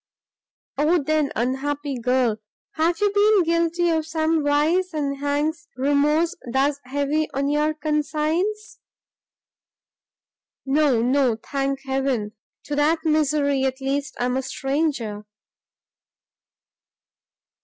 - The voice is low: No, very high, 290 Hz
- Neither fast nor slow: No, slow, 110 wpm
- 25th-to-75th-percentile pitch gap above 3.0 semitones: No, average, 2.7 semitones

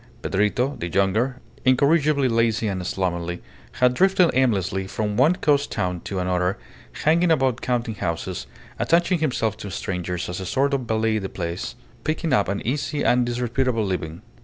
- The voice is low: Yes, low, 115 Hz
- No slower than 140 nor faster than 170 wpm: Yes, average, 160 wpm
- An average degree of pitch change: No, wide, 6.0 semitones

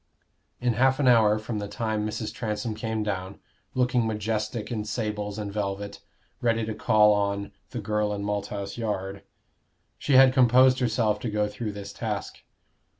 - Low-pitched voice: Yes, low, 105 Hz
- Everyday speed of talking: Yes, average, 160 wpm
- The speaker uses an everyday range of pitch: No, narrow, 2.0 semitones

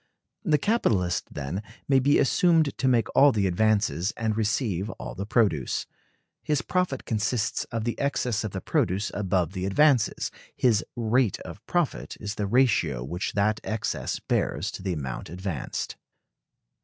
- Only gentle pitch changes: No, average, 5.3 semitones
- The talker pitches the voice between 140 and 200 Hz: No, low, 110 Hz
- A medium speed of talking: Yes, average, 155 wpm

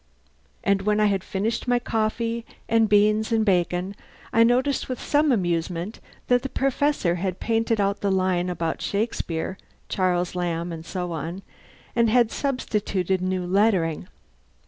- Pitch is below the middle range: No, high, 200 Hz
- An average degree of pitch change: Yes, average, 4.2 semitones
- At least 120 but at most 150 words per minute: Yes, average, 145 wpm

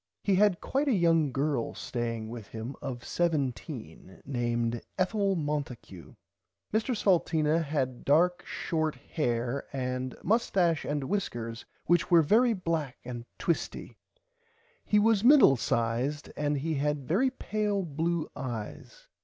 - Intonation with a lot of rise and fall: Yes, wide, 6.5 semitones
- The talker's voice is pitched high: No, medium, 150 Hz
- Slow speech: Yes, slow, 130 wpm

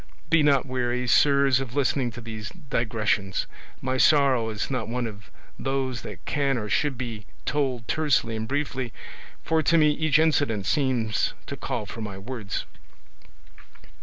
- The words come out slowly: No, average, 155 wpm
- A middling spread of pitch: Yes, average, 4.1 semitones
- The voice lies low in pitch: Yes, low, 130 Hz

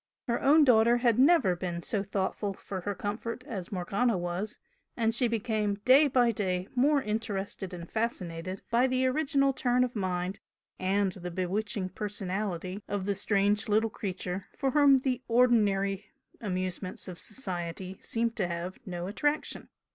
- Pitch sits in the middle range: No, high, 205 Hz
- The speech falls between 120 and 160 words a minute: Yes, average, 155 wpm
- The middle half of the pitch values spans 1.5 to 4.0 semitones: No, average, 4.4 semitones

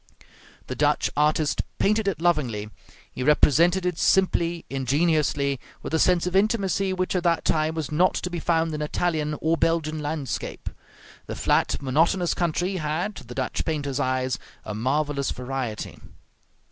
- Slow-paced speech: No, average, 155 wpm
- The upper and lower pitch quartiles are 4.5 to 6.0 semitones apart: No, average, 3.9 semitones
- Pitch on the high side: No, medium, 155 Hz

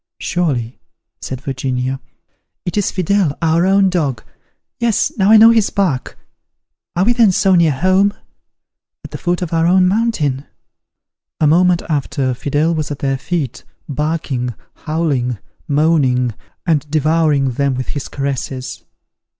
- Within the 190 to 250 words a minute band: No, average, 140 wpm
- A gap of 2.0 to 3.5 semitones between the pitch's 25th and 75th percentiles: No, average, 5.2 semitones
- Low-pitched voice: No, medium, 155 Hz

